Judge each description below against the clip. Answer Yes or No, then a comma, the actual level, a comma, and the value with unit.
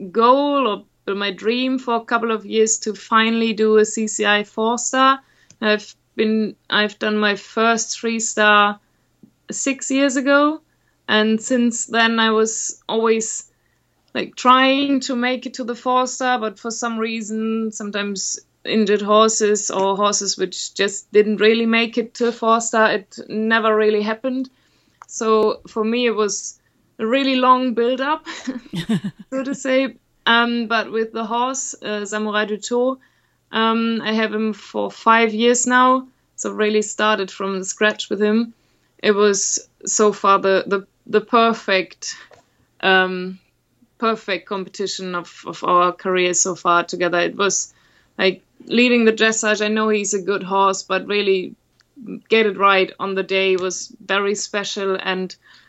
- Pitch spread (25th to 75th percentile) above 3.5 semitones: No, average, 2.8 semitones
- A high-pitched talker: Yes, high, 220 Hz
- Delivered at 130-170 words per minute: Yes, average, 155 wpm